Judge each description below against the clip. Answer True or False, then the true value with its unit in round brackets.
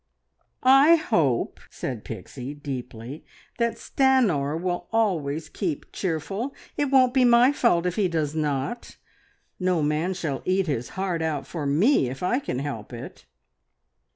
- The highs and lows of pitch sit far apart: True (8.1 semitones)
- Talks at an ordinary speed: True (145 wpm)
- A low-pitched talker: False (170 Hz)